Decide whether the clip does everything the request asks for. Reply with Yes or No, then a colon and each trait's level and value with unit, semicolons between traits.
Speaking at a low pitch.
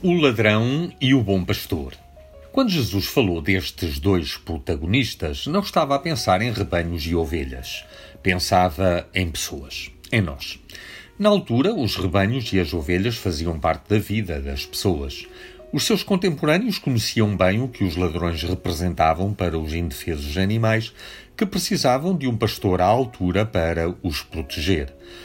Yes: very low, 95 Hz